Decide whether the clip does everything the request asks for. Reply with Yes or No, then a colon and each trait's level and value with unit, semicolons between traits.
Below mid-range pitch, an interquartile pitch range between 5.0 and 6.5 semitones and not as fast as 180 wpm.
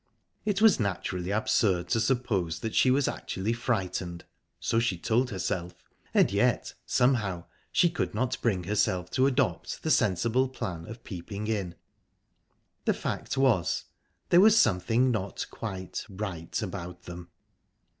Yes: low, 105 Hz; average, 5.3 semitones; slow, 135 wpm